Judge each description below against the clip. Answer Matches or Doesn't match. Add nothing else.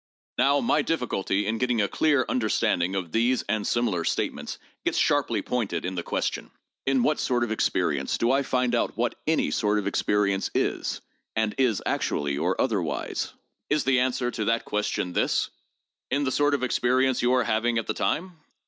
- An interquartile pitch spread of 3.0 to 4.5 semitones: Matches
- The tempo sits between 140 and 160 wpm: Doesn't match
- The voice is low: Matches